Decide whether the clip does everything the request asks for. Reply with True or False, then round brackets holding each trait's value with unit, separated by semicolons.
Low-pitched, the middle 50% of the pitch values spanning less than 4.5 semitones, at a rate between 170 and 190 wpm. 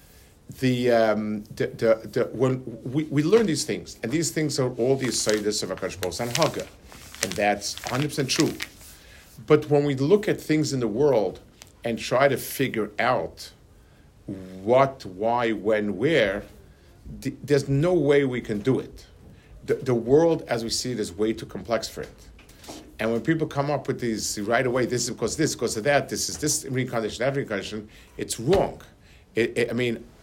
False (120 Hz; 4.8 semitones; 185 wpm)